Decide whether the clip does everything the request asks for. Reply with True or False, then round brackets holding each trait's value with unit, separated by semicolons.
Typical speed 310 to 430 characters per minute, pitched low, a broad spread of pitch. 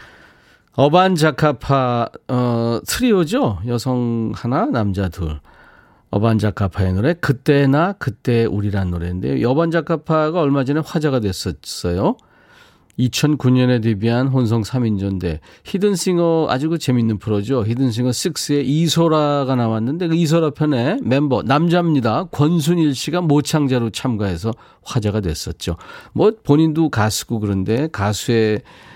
False (285 characters per minute; 125 Hz; 5.8 semitones)